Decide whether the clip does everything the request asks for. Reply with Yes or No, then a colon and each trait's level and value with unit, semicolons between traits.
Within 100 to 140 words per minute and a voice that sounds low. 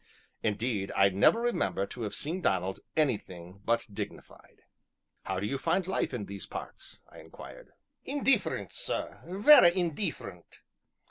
Yes: slow, 135 wpm; low, 120 Hz